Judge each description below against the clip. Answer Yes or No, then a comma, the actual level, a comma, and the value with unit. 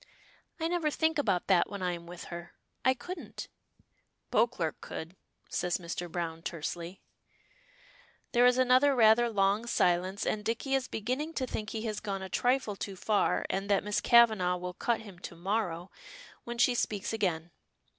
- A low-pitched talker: No, high, 205 Hz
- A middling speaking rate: Yes, average, 165 wpm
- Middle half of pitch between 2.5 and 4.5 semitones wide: No, average, 5.2 semitones